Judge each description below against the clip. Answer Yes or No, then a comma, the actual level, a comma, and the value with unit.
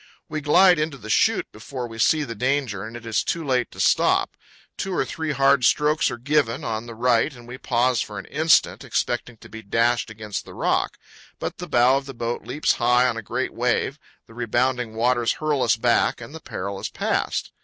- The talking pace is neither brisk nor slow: No, fast, 215 wpm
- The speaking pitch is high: No, low, 125 Hz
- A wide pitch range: No, average, 3.5 semitones